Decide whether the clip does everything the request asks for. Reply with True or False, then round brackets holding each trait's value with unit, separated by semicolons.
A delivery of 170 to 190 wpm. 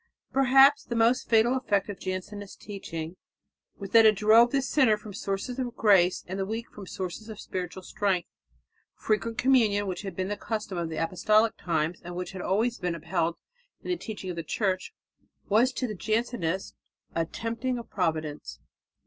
True (185 wpm)